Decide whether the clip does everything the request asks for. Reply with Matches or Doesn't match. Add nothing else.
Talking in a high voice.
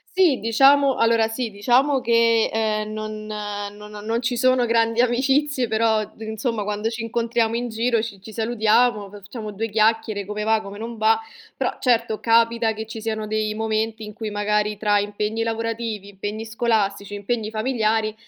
Matches